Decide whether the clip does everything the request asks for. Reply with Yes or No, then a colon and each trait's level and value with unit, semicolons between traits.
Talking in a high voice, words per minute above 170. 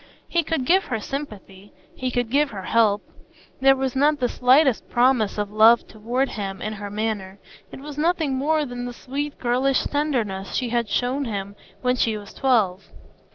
Yes: high, 245 Hz; average, 180 wpm